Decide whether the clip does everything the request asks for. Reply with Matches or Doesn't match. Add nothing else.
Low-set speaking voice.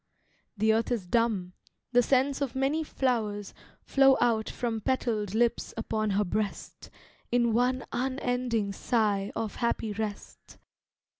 Doesn't match